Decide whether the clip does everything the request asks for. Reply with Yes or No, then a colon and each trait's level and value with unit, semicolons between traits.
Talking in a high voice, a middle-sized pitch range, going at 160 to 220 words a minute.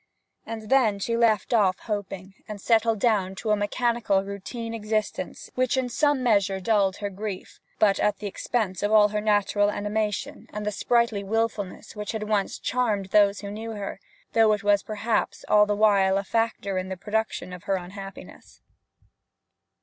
No: high, 210 Hz; narrow, 2.1 semitones; average, 175 wpm